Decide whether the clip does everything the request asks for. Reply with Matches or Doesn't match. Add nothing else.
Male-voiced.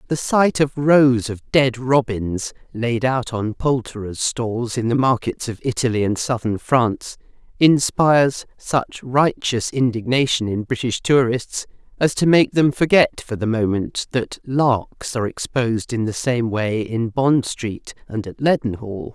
Doesn't match